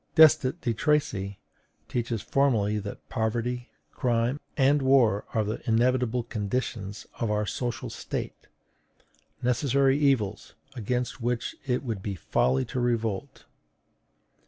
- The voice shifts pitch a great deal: No, average, 3.3 semitones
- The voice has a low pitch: Yes, low, 120 Hz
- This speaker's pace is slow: Yes, slow, 115 wpm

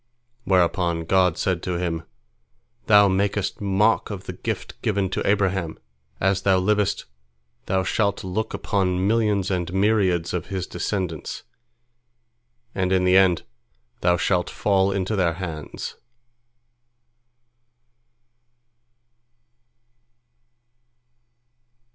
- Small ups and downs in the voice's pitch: Yes, narrow, 1.9 semitones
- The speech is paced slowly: Yes, slow, 100 wpm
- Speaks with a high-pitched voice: No, very low, 95 Hz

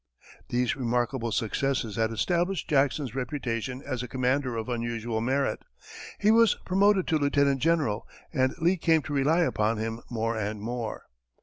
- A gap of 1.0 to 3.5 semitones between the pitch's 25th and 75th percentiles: No, average, 4.5 semitones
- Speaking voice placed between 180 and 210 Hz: No, low, 130 Hz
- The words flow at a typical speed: Yes, average, 150 wpm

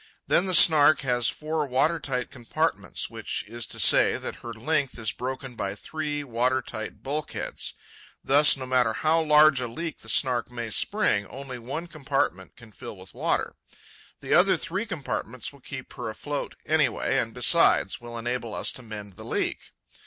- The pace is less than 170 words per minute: No, average, 175 wpm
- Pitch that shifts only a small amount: No, average, 4.5 semitones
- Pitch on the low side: Yes, low, 130 Hz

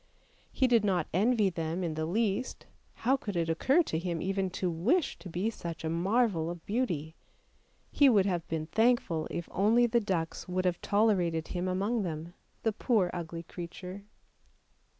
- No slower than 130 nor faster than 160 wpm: No, average, 175 wpm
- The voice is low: No, medium, 185 Hz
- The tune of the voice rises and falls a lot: No, average, 4.7 semitones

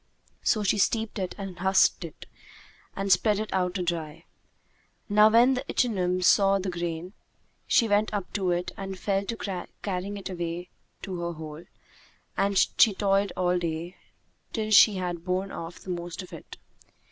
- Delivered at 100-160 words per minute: No, average, 170 wpm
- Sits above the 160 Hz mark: Yes, high, 190 Hz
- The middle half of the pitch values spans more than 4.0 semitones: No, narrow, 2.5 semitones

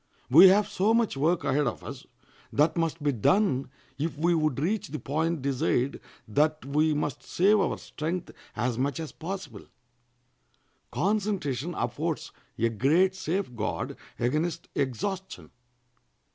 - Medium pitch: Yes, medium, 155 Hz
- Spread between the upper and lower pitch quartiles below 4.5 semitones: No, average, 5.2 semitones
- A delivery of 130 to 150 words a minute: Yes, slow, 135 wpm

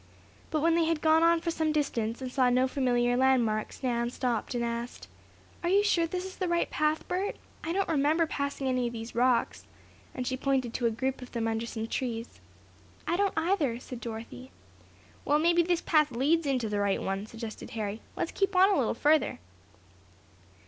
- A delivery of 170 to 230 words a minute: Yes, average, 195 wpm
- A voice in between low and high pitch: No, very high, 265 Hz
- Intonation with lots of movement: Yes, wide, 5.7 semitones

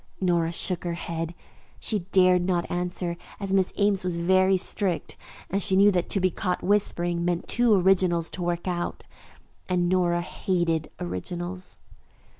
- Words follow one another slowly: No, average, 155 wpm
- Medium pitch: Yes, medium, 180 Hz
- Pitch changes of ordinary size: No, narrow, 1.5 semitones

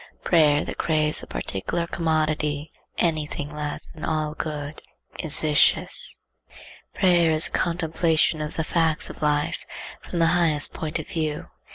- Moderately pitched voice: Yes, medium, 155 Hz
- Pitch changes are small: Yes, narrow, 1.5 semitones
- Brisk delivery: No, average, 150 wpm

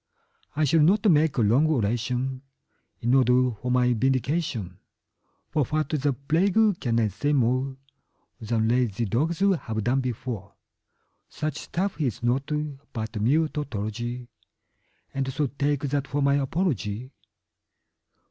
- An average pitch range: Yes, average, 4.0 semitones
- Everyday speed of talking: No, slow, 130 wpm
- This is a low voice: Yes, low, 130 Hz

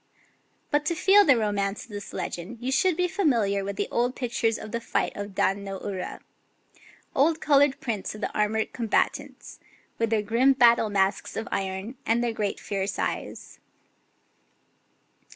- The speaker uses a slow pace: No, average, 165 wpm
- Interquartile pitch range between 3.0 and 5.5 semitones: Yes, average, 4.3 semitones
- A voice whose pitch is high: Yes, high, 225 Hz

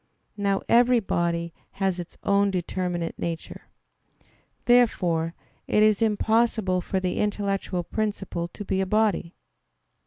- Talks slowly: Yes, slow, 120 wpm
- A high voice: Yes, high, 195 Hz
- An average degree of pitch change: Yes, average, 3.4 semitones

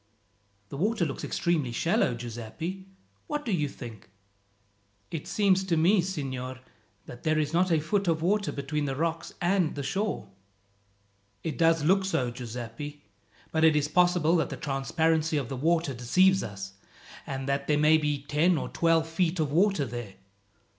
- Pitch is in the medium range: Yes, medium, 155 Hz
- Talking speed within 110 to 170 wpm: Yes, average, 165 wpm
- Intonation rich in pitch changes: No, average, 4.3 semitones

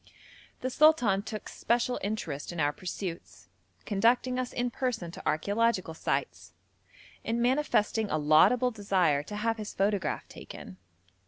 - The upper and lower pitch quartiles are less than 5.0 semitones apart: No, wide, 5.5 semitones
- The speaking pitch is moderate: No, high, 210 Hz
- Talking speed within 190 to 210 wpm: No, slow, 135 wpm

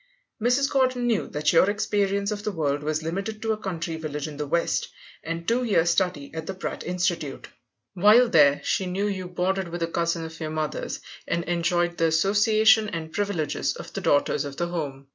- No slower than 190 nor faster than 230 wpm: Yes, average, 200 wpm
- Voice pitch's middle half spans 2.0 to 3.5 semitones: No, average, 4.2 semitones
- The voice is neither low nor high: Yes, medium, 175 Hz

